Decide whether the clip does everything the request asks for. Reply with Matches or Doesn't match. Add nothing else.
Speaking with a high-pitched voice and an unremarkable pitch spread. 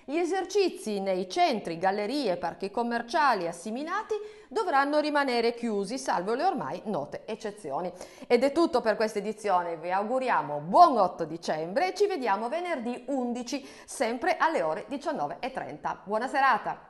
Doesn't match